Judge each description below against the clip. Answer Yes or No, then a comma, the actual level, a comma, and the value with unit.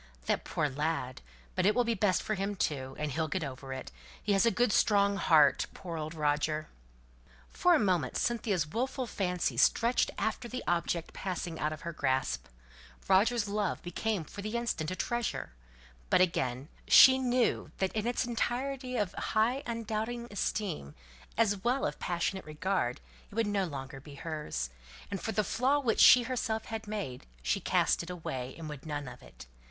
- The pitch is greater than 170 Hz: Yes, high, 190 Hz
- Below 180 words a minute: No, average, 185 wpm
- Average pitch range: No, wide, 6.9 semitones